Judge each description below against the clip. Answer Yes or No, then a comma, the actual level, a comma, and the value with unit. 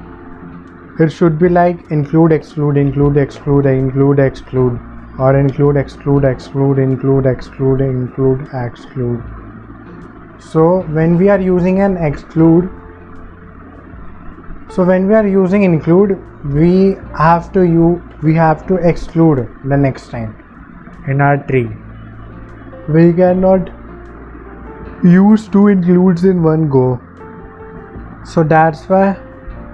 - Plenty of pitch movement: Yes, wide, 7.0 semitones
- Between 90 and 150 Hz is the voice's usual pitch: Yes, medium, 140 Hz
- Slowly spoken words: Yes, slow, 115 wpm